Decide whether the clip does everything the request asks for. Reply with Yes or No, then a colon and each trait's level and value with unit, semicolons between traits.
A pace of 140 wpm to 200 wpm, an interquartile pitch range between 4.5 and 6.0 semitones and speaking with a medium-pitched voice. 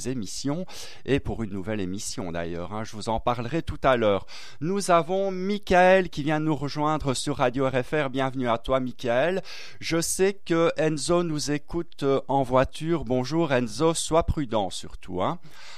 Yes: average, 165 wpm; average, 5.2 semitones; medium, 145 Hz